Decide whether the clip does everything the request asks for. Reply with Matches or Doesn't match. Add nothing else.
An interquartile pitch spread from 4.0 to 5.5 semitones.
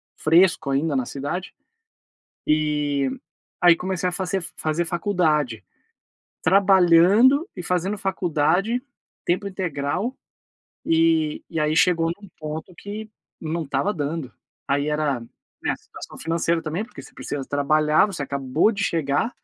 Matches